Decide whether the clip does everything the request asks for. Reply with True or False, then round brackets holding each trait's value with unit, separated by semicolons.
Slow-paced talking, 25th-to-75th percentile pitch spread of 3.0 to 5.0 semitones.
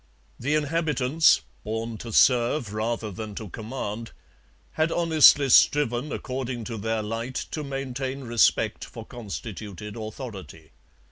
True (120 wpm; 3.9 semitones)